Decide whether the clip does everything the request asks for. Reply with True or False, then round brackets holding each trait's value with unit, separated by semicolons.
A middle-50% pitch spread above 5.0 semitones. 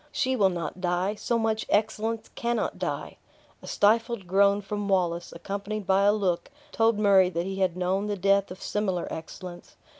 False (2.6 semitones)